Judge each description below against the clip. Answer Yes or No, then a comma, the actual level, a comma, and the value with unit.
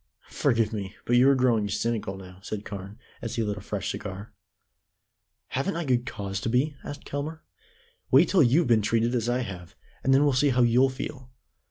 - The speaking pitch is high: No, low, 120 Hz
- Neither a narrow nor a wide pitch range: Yes, average, 4.4 semitones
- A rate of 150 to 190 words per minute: No, average, 200 wpm